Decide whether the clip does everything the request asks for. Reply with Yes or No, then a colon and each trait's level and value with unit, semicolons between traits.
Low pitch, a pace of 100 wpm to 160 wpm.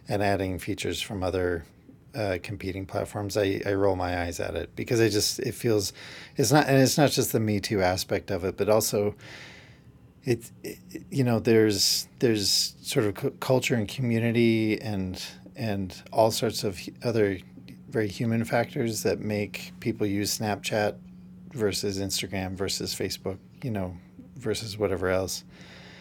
Yes: low, 105 Hz; average, 155 wpm